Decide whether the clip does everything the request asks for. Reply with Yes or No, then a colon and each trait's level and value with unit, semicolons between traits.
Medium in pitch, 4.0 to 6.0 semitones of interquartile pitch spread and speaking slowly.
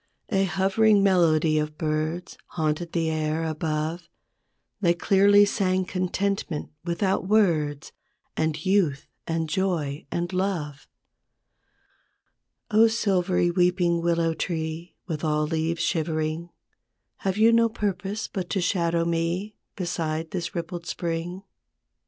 No: medium, 170 Hz; average, 3.1 semitones; slow, 115 wpm